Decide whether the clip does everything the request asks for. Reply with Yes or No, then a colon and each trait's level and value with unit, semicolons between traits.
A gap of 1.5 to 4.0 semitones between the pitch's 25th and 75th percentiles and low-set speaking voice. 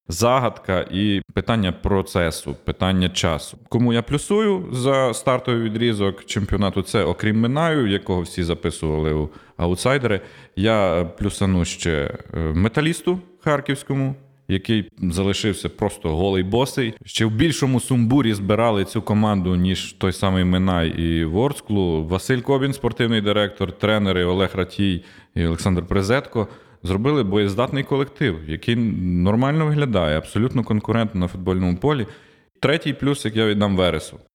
No: average, 5.1 semitones; low, 105 Hz